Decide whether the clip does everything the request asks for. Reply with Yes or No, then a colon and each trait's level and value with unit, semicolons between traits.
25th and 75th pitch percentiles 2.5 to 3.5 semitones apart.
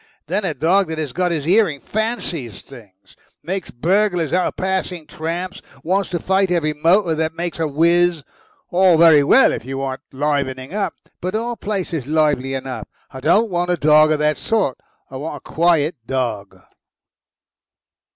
No: average, 4.2 semitones